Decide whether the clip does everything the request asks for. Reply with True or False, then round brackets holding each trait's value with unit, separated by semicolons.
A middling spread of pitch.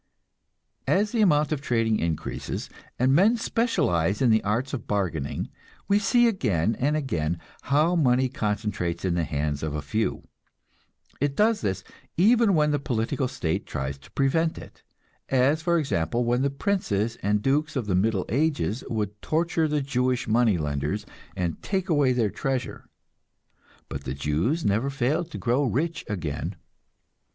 False (7.8 semitones)